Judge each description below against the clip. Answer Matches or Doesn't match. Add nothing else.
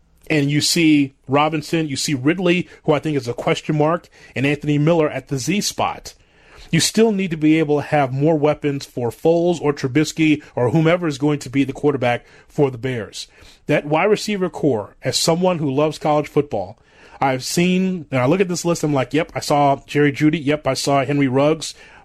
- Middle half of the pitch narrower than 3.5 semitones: Matches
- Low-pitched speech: Doesn't match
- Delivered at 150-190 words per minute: Doesn't match